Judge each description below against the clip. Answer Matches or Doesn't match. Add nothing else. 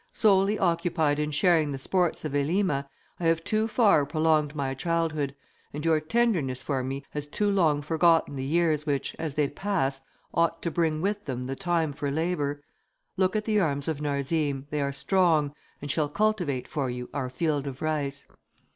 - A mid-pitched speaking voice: Matches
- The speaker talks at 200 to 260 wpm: Doesn't match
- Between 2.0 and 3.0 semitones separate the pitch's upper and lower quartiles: Doesn't match